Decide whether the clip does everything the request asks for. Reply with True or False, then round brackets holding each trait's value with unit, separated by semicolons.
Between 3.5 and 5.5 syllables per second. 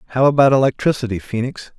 False (6.8 syllables/s)